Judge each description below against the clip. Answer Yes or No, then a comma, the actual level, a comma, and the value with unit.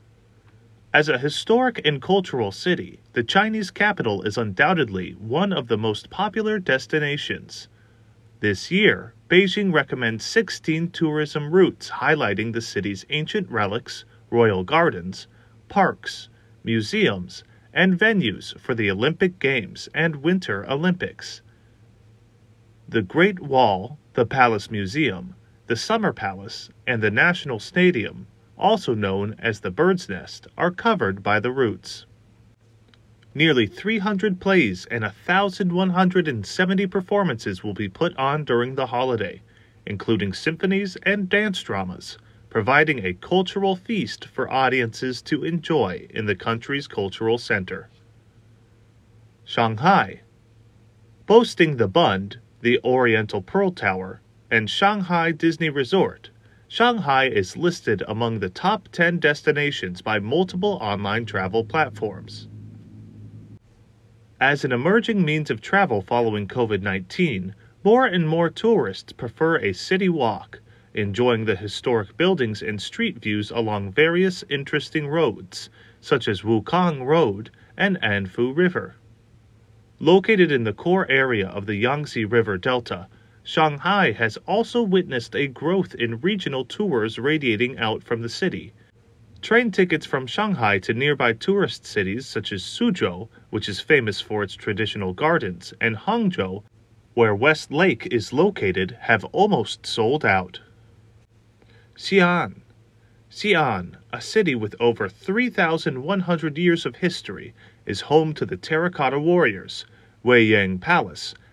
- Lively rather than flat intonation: Yes, wide, 7.6 semitones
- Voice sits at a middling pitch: No, low, 115 Hz